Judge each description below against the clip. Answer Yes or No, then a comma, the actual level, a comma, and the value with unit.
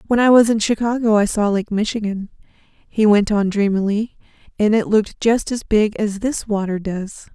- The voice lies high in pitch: Yes, high, 210 Hz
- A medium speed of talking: Yes, average, 190 wpm